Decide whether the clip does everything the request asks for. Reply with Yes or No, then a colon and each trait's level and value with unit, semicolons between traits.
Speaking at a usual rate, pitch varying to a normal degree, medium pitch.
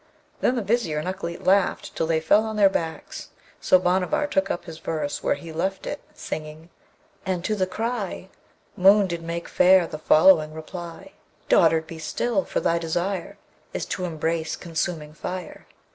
Yes: average, 170 wpm; average, 3.1 semitones; medium, 175 Hz